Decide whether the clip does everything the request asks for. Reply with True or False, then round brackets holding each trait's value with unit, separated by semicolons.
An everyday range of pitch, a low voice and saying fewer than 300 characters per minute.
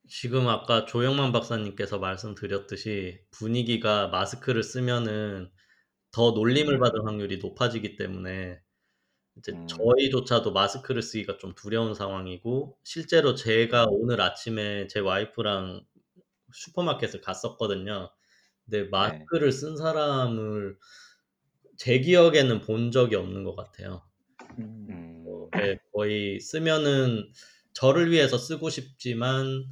True (4.6 semitones; 115 Hz; 265 characters per minute)